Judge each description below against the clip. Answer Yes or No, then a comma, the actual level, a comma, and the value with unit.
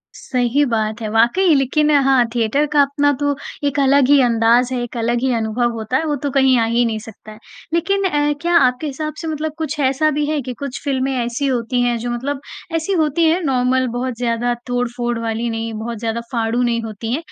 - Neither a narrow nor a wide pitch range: Yes, average, 3.6 semitones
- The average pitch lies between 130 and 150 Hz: No, very high, 255 Hz